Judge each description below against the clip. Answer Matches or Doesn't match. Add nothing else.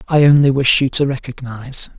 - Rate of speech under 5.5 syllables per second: Doesn't match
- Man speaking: Matches